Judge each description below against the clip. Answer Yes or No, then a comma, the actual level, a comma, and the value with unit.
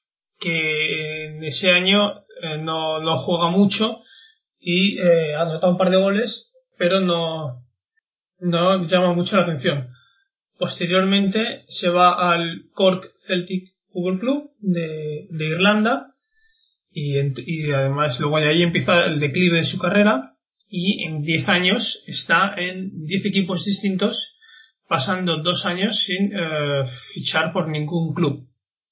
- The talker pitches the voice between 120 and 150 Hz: No, medium, 180 Hz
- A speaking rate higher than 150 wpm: No, average, 135 wpm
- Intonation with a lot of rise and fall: No, average, 3.8 semitones